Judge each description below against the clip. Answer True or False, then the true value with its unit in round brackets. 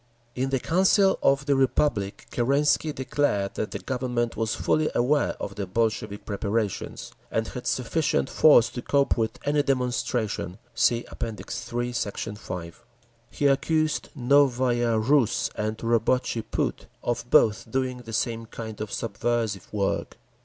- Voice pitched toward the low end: True (120 Hz)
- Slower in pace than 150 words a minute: True (140 wpm)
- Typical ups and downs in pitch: True (3.7 semitones)